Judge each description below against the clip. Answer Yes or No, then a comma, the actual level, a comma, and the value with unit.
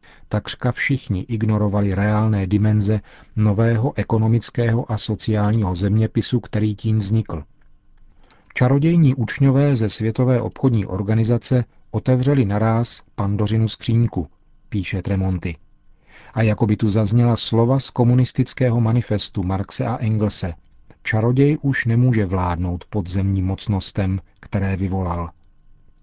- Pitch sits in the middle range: No, low, 110 Hz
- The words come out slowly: Yes, slow, 105 wpm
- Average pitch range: Yes, average, 3.2 semitones